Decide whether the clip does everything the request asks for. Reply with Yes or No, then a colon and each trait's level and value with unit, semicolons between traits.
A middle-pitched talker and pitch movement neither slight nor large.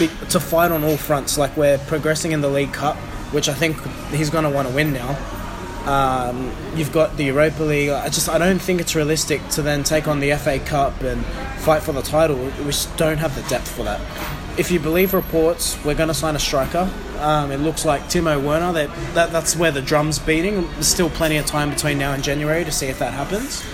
No: medium, 150 Hz; narrow, 2.1 semitones